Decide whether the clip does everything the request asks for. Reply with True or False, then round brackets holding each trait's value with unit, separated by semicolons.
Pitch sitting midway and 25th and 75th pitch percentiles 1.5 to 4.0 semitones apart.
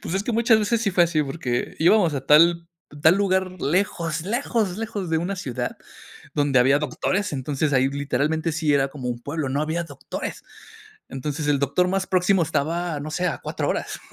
False (160 Hz; 4.5 semitones)